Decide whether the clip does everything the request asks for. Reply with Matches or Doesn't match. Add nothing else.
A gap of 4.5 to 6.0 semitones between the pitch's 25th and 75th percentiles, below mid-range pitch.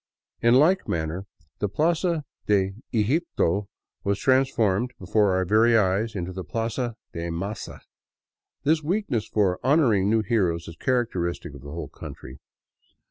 Matches